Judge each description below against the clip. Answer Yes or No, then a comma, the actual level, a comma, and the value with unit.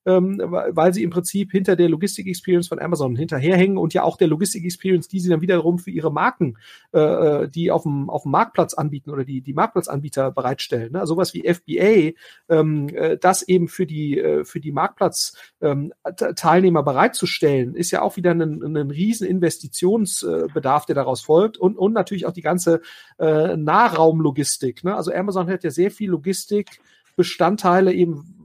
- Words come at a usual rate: Yes, average, 150 wpm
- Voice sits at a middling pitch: Yes, medium, 175 Hz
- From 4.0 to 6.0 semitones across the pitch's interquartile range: No, average, 3.2 semitones